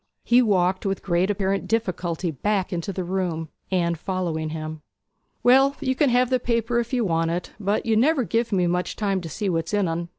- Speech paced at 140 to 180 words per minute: No, fast, 205 wpm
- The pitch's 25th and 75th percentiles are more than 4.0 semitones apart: Yes, average, 4.9 semitones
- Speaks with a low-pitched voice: No, high, 190 Hz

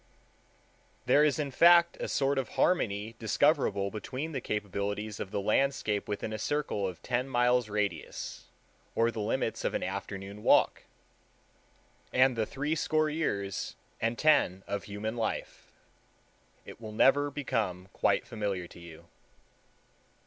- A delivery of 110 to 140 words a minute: Yes, slow, 135 wpm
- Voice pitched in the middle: No, low, 110 Hz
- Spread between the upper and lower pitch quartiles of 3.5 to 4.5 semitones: No, average, 5.2 semitones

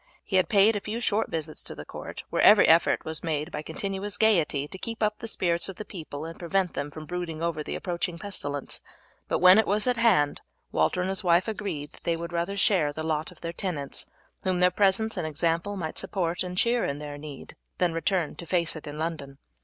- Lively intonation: No, average, 3.8 semitones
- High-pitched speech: No, medium, 175 Hz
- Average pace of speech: No, fast, 230 wpm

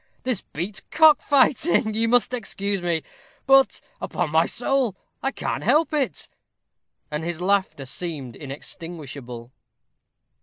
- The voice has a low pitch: No, high, 190 Hz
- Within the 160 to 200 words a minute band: No, average, 140 wpm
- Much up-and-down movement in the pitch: Yes, wide, 8.1 semitones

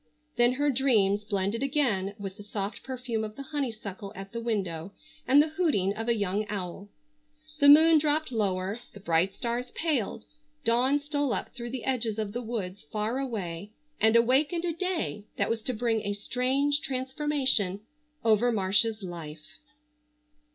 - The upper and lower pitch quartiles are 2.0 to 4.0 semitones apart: No, average, 4.9 semitones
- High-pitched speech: Yes, high, 230 Hz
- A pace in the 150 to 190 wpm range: Yes, average, 160 wpm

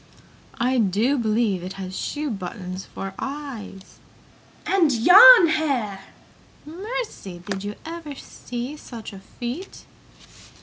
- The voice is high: Yes, high, 240 Hz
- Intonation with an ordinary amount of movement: No, wide, 7.6 semitones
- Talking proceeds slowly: Yes, slow, 105 wpm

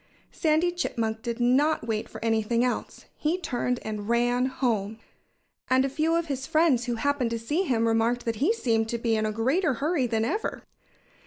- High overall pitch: Yes, high, 245 Hz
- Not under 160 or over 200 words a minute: Yes, average, 190 wpm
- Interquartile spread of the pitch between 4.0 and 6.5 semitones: Yes, average, 4.5 semitones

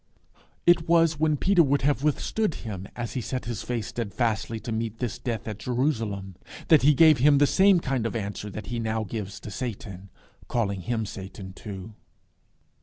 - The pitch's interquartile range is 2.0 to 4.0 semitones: No, average, 5.3 semitones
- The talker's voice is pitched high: No, low, 115 Hz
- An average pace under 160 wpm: No, average, 180 wpm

